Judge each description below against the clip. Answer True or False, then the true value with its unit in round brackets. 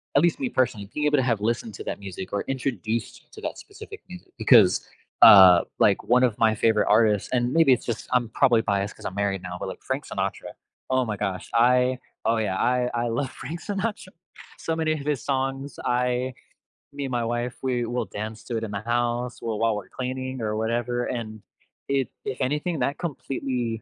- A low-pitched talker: True (120 Hz)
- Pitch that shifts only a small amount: False (3.1 semitones)